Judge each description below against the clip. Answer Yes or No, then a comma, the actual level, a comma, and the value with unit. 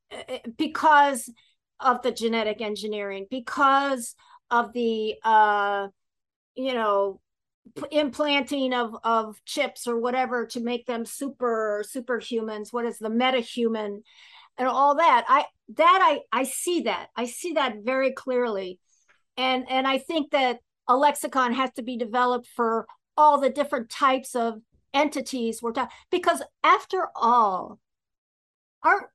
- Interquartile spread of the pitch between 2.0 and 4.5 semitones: Yes, average, 3.6 semitones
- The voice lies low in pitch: No, very high, 250 Hz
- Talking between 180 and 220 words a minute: No, slow, 135 wpm